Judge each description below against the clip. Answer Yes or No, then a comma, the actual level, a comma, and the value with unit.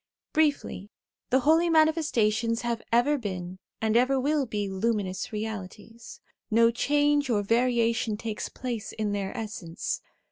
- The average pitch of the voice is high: Yes, high, 230 Hz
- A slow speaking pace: Yes, slow, 130 wpm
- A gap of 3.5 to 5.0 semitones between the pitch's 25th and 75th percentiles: Yes, average, 4.0 semitones